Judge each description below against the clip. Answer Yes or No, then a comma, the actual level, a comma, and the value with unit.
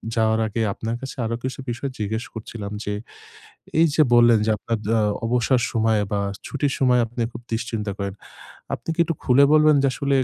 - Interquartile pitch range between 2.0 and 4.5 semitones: Yes, average, 3.2 semitones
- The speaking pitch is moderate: No, low, 115 Hz